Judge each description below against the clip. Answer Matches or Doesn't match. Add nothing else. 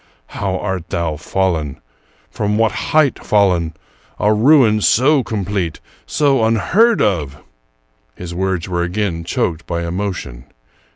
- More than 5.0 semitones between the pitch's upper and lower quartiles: Doesn't match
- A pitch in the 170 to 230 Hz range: Doesn't match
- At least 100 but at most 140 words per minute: Matches